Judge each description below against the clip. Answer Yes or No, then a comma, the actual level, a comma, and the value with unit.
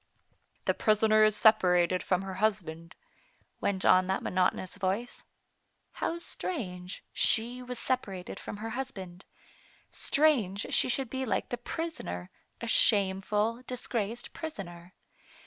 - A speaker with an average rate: No, slow, 125 wpm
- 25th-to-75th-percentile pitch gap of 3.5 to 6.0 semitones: Yes, average, 4.6 semitones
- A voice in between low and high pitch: No, high, 210 Hz